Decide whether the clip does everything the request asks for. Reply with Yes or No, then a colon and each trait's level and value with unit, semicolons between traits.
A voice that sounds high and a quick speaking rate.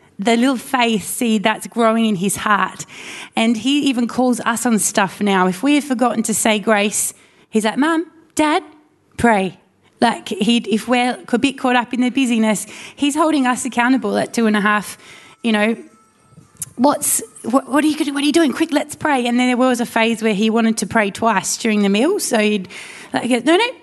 Yes: high, 235 Hz; fast, 210 wpm